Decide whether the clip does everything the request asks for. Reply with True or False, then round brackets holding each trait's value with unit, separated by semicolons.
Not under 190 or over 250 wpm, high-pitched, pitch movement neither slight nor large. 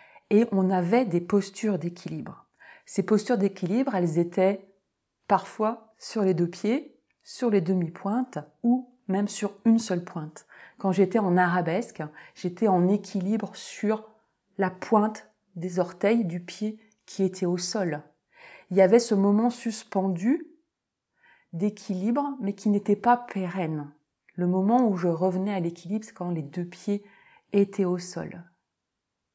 False (145 wpm; 195 Hz; 3.3 semitones)